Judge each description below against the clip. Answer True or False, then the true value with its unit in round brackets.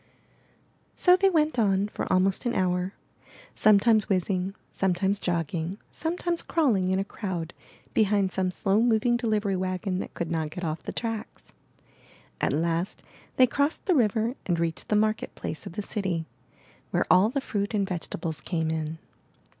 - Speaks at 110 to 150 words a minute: False (160 wpm)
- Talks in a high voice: True (195 Hz)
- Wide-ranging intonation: False (3.8 semitones)